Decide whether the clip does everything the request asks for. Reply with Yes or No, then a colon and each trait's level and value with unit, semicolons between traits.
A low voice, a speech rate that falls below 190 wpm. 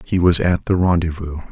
No: very low, 85 Hz; average, 200 wpm